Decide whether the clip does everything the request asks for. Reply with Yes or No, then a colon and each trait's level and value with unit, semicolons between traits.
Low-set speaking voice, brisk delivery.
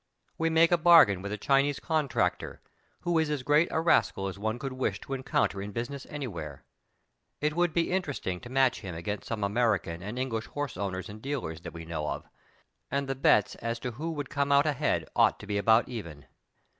Yes: low, 125 Hz; fast, 210 wpm